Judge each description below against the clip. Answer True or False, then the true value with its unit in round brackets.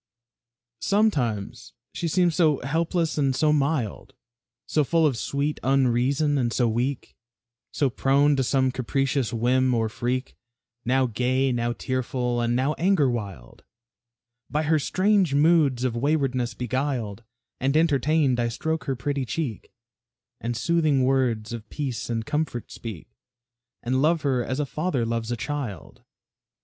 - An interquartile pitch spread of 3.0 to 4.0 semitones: True (3.7 semitones)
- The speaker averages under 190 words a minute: True (140 wpm)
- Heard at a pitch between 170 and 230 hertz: False (130 Hz)